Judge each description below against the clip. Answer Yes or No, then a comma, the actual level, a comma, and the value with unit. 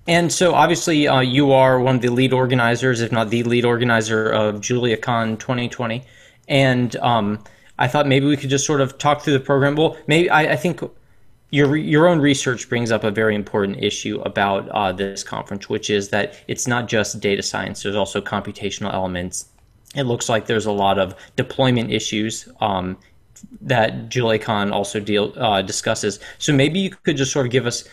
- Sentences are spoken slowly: No, average, 190 wpm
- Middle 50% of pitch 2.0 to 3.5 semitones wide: No, average, 4.4 semitones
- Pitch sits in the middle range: No, low, 120 Hz